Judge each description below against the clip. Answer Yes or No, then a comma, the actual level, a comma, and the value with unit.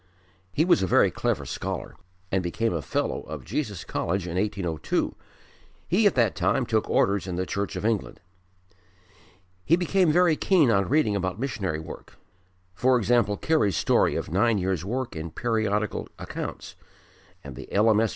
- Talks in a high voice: No, low, 105 Hz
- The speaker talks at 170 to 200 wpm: No, average, 160 wpm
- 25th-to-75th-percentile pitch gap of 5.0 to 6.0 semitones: Yes, wide, 5.4 semitones